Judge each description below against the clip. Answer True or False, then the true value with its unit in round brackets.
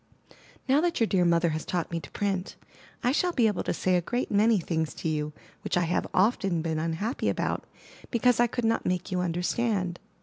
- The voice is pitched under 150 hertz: False (185 Hz)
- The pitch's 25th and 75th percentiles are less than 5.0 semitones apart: False (5.3 semitones)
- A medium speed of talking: False (210 wpm)